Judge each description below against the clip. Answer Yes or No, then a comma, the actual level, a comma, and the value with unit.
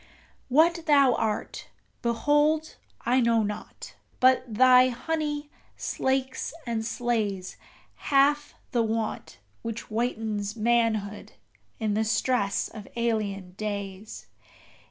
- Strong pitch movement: No, average, 3.5 semitones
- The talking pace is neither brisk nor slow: No, slow, 100 wpm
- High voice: Yes, high, 235 Hz